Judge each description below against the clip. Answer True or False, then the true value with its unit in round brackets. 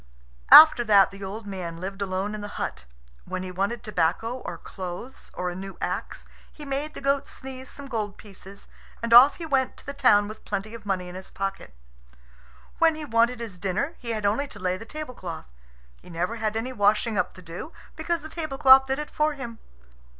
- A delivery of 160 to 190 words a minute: False (205 wpm)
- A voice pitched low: False (215 Hz)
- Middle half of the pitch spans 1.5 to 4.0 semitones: False (5.6 semitones)